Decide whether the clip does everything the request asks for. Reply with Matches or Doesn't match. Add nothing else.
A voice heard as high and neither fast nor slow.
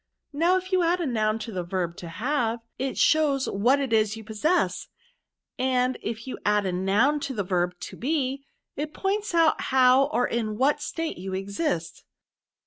Matches